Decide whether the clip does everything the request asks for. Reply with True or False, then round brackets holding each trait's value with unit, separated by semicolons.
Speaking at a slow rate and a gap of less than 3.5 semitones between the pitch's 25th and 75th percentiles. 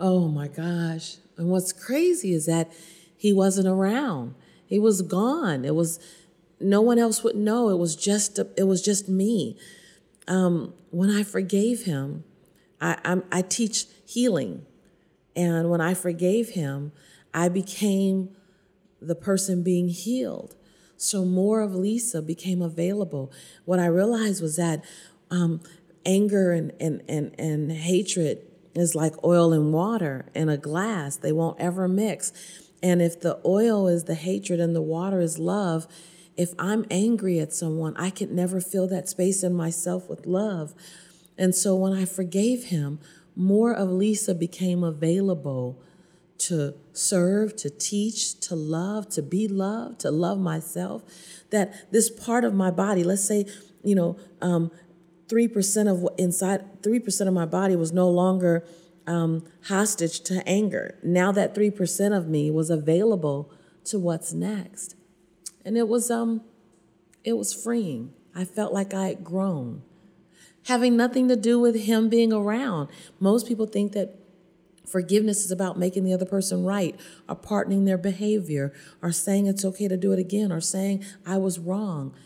False (160 wpm; 2.9 semitones)